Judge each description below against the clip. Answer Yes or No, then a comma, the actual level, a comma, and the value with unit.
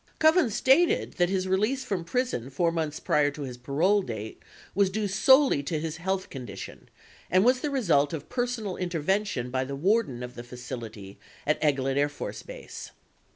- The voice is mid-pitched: Yes, medium, 170 Hz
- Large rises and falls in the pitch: Yes, wide, 7.6 semitones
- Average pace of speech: Yes, average, 180 wpm